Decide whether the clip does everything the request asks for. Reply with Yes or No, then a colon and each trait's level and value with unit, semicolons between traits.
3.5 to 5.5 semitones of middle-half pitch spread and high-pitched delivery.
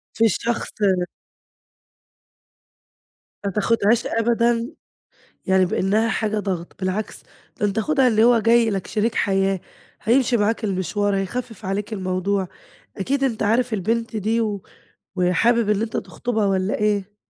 No: average, 2.9 semitones; high, 210 Hz